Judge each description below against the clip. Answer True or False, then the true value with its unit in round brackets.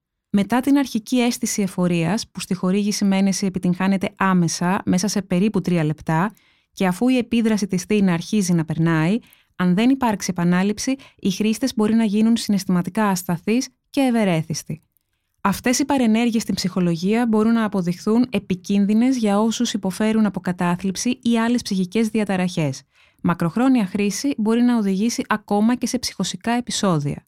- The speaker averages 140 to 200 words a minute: True (145 wpm)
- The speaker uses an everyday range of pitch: True (3.8 semitones)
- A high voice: True (205 Hz)